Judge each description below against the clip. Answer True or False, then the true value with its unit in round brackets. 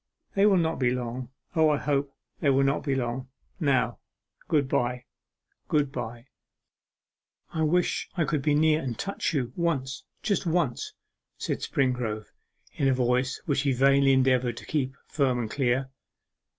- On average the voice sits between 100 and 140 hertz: True (135 Hz)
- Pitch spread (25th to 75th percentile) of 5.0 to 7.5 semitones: False (3.3 semitones)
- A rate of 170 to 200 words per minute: False (160 wpm)